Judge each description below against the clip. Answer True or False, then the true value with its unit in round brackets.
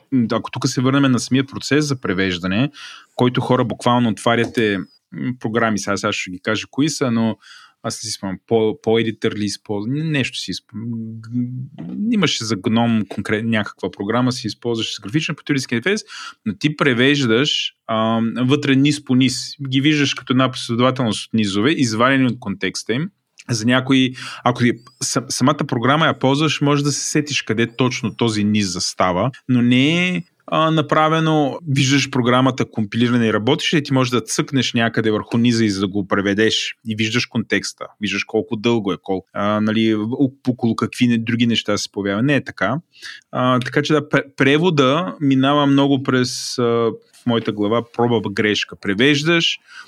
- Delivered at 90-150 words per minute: False (165 wpm)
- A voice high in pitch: False (125 Hz)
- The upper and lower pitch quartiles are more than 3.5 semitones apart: True (3.9 semitones)